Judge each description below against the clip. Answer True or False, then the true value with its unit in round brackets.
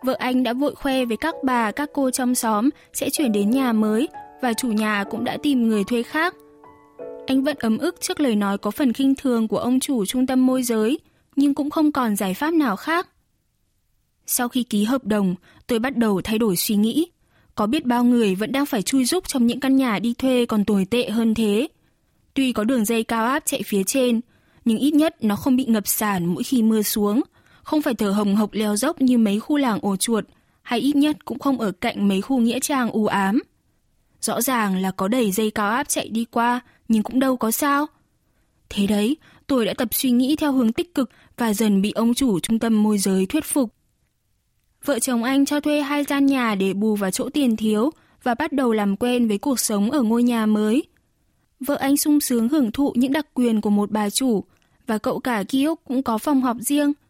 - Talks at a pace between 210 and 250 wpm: True (230 wpm)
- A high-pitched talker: True (245 Hz)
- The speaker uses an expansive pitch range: False (4.2 semitones)